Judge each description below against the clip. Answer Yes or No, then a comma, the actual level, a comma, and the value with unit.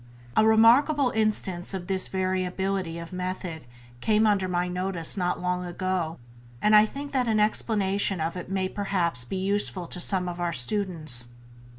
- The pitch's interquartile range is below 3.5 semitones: Yes, average, 2.9 semitones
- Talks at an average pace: Yes, average, 165 wpm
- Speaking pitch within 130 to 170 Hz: No, medium, 185 Hz